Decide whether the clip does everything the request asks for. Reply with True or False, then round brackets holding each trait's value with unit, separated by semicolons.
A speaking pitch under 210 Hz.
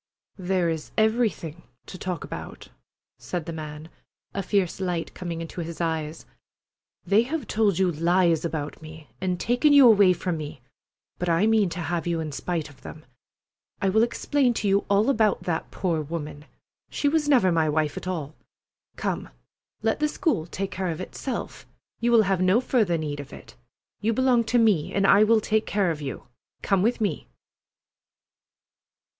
True (185 Hz)